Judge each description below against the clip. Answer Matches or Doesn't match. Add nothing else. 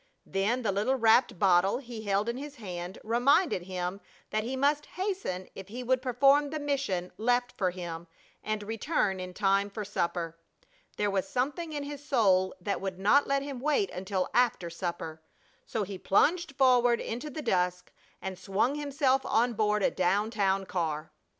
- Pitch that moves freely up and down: Matches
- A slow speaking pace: Doesn't match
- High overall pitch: Matches